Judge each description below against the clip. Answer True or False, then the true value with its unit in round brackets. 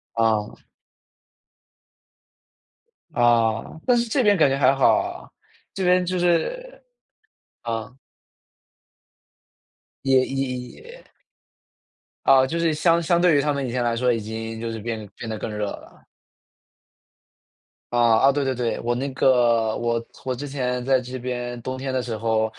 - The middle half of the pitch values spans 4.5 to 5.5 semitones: False (3.7 semitones)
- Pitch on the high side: False (125 Hz)